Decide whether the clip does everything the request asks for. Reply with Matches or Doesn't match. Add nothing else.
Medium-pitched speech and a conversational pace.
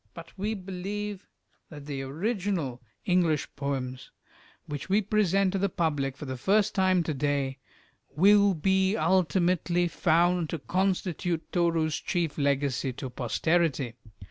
Doesn't match